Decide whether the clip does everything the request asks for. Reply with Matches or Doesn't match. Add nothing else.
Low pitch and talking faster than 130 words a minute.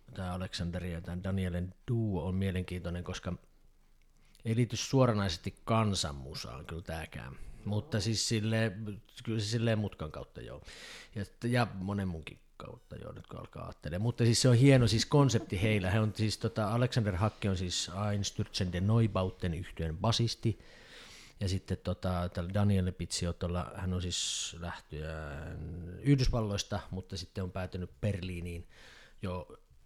Matches